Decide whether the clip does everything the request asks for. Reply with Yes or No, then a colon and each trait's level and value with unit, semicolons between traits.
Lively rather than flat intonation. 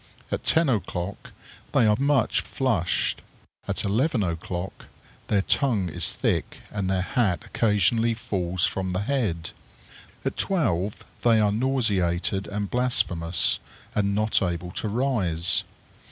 No: average, 4.7 semitones